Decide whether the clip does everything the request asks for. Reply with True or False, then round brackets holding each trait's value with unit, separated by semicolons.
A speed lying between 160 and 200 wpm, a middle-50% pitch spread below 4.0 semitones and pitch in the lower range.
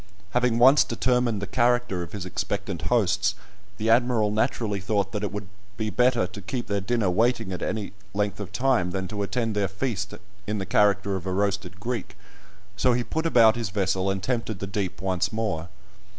True (190 wpm; 3.4 semitones; 105 Hz)